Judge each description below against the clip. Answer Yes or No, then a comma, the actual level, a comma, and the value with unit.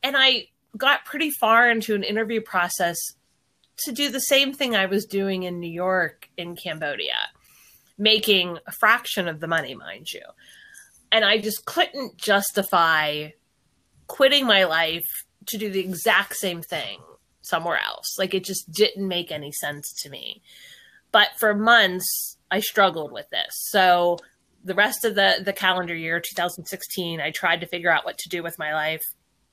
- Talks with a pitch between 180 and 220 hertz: Yes, high, 190 Hz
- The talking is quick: No, average, 165 wpm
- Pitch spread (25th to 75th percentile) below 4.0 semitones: No, average, 4.3 semitones